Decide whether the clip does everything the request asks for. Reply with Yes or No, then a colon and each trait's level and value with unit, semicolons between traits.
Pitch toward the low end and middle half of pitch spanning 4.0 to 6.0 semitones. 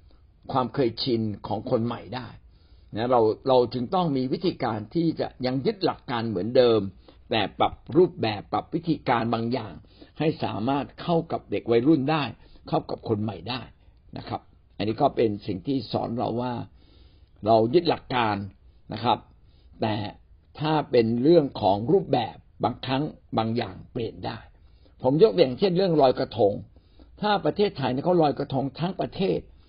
Yes: low, 120 Hz; wide, 5.4 semitones